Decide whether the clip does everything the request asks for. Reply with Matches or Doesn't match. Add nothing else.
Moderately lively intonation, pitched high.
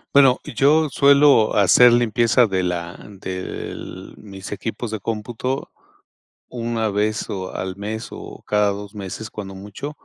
Doesn't match